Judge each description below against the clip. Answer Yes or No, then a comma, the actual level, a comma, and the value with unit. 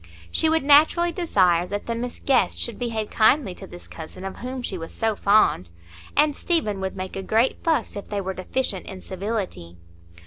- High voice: Yes, high, 215 Hz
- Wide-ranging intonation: Yes, wide, 5.7 semitones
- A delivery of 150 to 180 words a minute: No, average, 195 wpm